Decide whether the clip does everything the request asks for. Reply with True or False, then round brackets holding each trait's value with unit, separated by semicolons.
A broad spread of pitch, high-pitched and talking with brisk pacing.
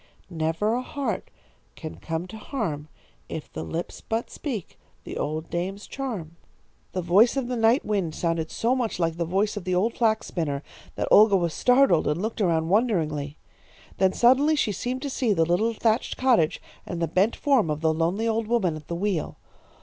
False (5.8 semitones; 195 Hz; 190 wpm)